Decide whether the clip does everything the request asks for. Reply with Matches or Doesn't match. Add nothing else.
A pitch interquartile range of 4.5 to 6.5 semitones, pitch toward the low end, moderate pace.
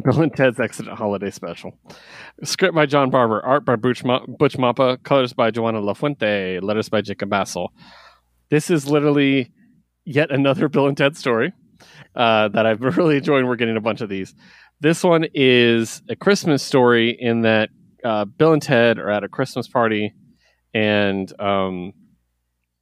Matches